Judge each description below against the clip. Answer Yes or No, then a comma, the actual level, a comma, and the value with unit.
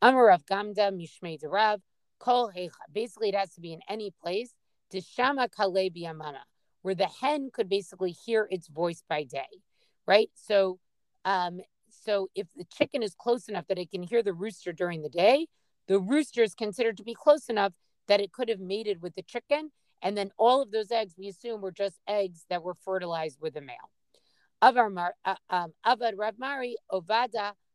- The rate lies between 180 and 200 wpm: No, average, 160 wpm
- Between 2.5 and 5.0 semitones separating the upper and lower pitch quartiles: Yes, average, 4.2 semitones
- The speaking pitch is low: No, high, 200 Hz